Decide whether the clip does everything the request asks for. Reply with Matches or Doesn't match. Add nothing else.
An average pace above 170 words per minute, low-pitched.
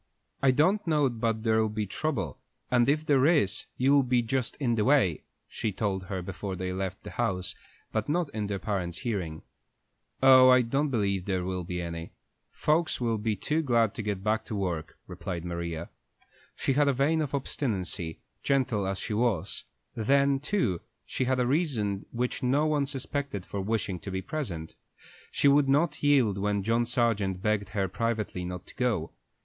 Matches